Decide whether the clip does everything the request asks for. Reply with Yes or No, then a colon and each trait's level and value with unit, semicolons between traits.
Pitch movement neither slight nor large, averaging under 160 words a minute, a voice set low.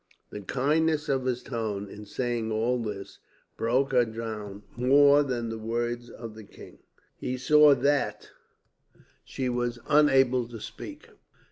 Yes: average, 3.0 semitones; average, 140 wpm; low, 120 Hz